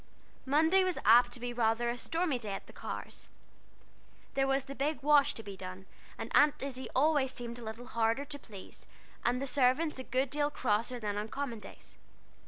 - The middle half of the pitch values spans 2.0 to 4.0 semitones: Yes, average, 3.7 semitones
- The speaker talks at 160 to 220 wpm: Yes, average, 195 wpm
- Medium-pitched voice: No, very high, 255 Hz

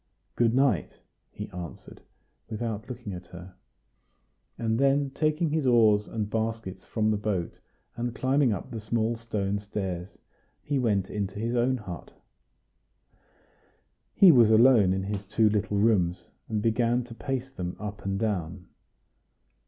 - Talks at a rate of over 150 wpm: No, average, 145 wpm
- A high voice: No, low, 110 Hz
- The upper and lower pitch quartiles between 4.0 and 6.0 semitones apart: No, average, 3.4 semitones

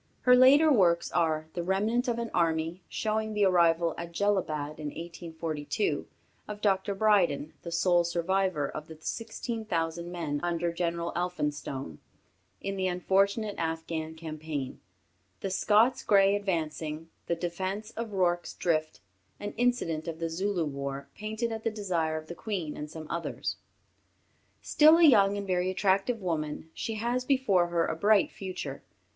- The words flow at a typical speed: Yes, average, 150 wpm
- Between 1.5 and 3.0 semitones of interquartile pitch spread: No, average, 4.2 semitones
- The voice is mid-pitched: Yes, medium, 175 Hz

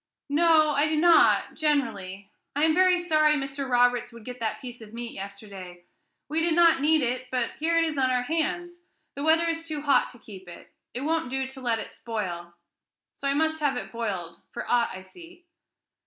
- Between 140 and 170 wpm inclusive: No, fast, 205 wpm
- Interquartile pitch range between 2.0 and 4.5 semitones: No, wide, 5.5 semitones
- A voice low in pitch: No, very high, 270 Hz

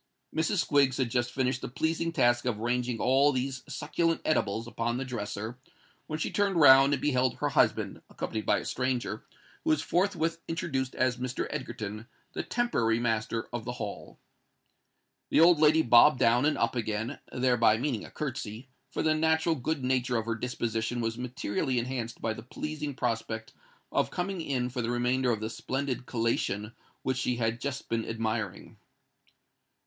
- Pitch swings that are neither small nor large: Yes, average, 3.6 semitones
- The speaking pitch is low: Yes, low, 125 Hz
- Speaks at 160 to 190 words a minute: Yes, average, 170 wpm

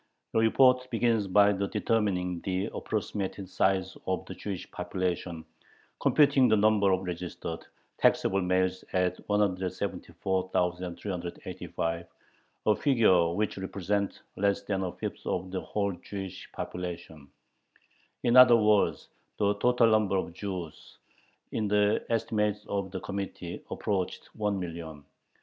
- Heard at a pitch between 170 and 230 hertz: No, very low, 95 Hz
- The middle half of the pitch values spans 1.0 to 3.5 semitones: Yes, narrow, 2.6 semitones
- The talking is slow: Yes, slow, 120 wpm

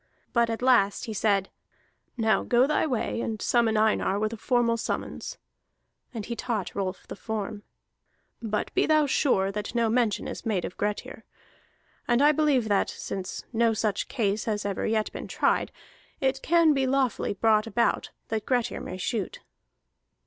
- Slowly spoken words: No, average, 165 wpm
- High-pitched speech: Yes, high, 225 Hz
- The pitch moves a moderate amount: Yes, average, 3.1 semitones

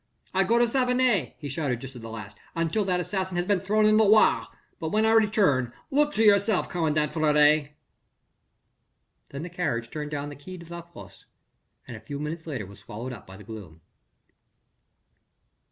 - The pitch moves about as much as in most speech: No, wide, 6.8 semitones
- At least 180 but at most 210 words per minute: Yes, average, 185 wpm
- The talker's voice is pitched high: No, medium, 165 Hz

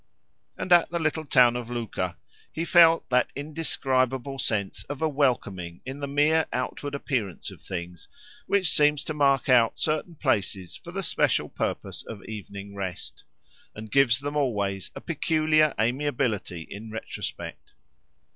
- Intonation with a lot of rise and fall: Yes, wide, 5.9 semitones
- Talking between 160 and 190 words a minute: No, average, 145 wpm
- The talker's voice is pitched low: Yes, low, 130 Hz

